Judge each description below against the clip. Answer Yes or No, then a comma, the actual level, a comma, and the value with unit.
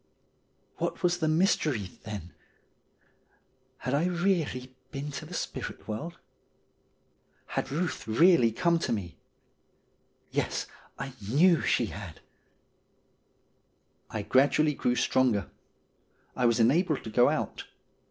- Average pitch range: No, wide, 6.8 semitones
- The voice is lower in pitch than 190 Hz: Yes, low, 135 Hz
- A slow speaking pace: Yes, slow, 115 wpm